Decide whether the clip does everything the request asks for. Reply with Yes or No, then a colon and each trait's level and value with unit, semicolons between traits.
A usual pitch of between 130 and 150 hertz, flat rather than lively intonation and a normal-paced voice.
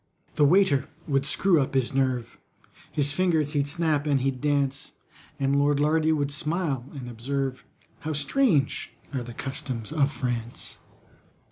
Yes: medium, 140 Hz; narrow, 2.3 semitones; average, 145 wpm